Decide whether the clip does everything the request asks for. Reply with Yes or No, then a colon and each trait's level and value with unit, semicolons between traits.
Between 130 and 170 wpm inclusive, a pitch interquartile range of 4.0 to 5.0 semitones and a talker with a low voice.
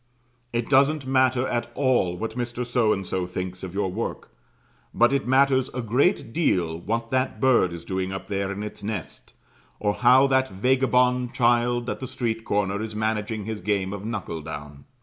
No: average, 185 wpm; average, 4.6 semitones; low, 115 Hz